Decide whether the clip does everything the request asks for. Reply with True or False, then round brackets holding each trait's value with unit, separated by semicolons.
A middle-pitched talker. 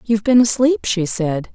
False (220 Hz)